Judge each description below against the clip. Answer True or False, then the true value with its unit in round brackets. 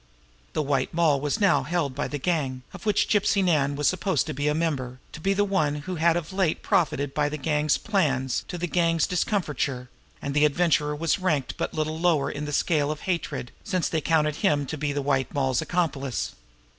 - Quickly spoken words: True (210 wpm)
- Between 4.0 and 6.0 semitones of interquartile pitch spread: False (3.4 semitones)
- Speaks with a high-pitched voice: False (150 Hz)